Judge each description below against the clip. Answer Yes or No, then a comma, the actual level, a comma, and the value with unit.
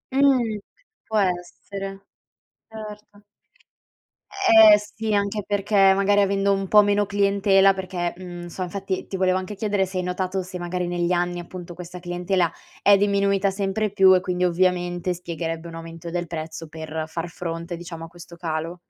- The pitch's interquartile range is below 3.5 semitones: Yes, narrow, 2.4 semitones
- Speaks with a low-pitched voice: No, medium, 185 Hz